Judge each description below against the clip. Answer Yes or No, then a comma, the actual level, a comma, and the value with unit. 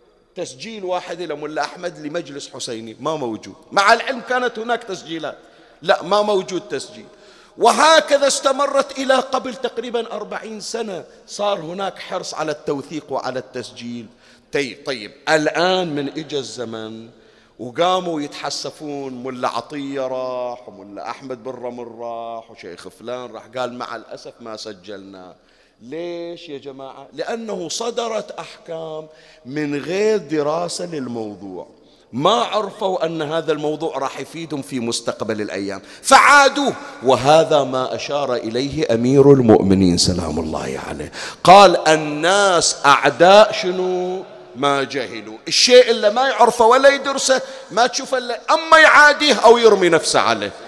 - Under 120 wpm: No, average, 125 wpm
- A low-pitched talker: No, medium, 155 Hz